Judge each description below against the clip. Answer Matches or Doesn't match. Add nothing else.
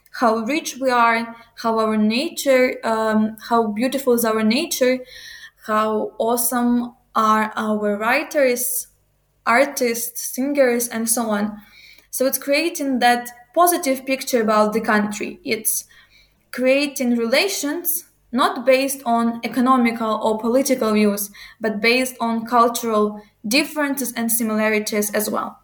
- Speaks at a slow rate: Matches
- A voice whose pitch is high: Matches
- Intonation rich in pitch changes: Doesn't match